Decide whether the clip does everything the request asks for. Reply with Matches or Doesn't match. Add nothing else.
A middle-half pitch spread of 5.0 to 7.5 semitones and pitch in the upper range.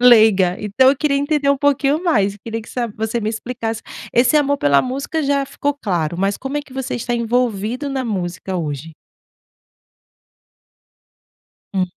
Matches